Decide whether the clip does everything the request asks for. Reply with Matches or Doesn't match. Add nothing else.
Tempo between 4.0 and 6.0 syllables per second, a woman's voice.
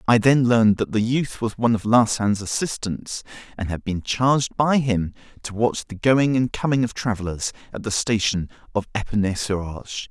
Doesn't match